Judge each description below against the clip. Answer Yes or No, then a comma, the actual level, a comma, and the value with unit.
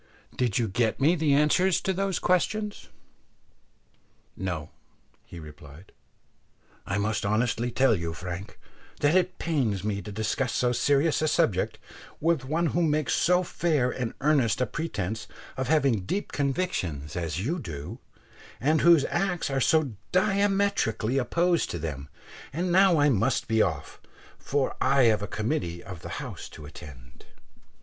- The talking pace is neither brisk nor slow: Yes, average, 150 wpm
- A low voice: Yes, low, 130 Hz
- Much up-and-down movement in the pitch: Yes, wide, 8.6 semitones